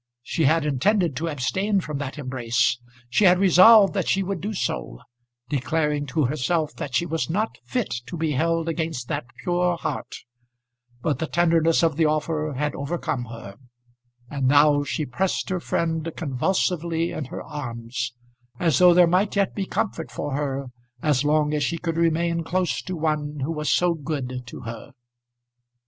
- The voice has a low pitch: No, medium, 160 Hz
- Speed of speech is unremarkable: Yes, average, 170 wpm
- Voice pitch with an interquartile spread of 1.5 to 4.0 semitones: Yes, average, 3.4 semitones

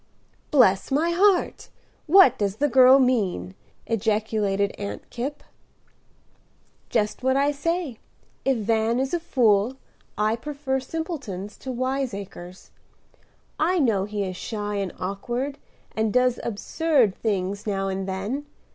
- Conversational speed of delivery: No, slow, 125 wpm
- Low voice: No, high, 230 Hz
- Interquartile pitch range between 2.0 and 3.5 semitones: No, average, 5.3 semitones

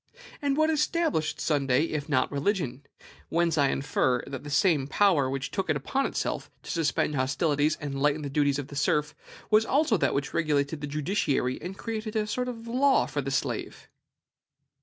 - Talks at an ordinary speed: Yes, average, 185 wpm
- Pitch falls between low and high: Yes, medium, 150 Hz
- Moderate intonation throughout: No, wide, 6.6 semitones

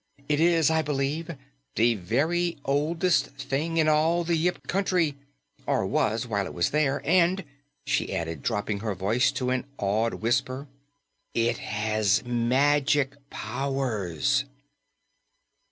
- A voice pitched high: No, low, 135 Hz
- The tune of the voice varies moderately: No, wide, 5.8 semitones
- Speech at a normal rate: No, slow, 125 wpm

